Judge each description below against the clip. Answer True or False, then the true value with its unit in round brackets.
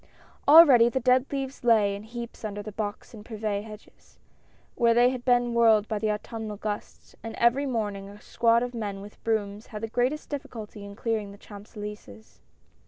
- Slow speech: False (190 wpm)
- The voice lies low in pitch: False (220 Hz)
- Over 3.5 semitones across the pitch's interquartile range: False (2.5 semitones)